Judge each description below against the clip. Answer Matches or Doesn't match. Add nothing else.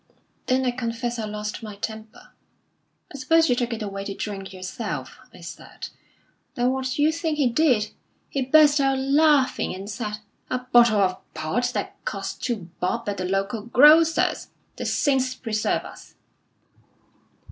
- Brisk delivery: Doesn't match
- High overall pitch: Matches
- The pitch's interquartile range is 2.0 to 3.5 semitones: Doesn't match